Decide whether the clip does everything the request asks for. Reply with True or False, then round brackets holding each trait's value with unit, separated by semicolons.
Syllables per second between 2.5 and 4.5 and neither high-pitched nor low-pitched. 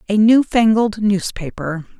False (4.1 syllables/s; 205 Hz)